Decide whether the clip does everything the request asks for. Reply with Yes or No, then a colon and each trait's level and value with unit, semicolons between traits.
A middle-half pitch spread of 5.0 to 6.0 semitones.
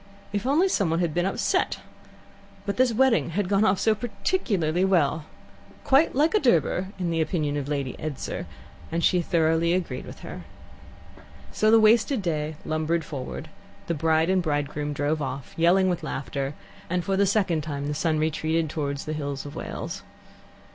No: average, 4.6 semitones